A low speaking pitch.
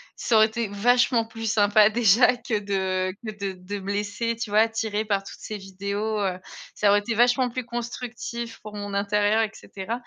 No: high, 215 Hz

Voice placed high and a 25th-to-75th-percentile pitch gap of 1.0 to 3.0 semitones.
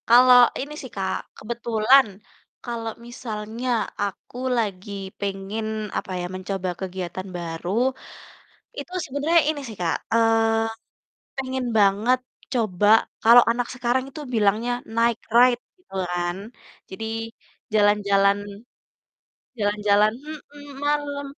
No: high, 225 Hz; average, 3.8 semitones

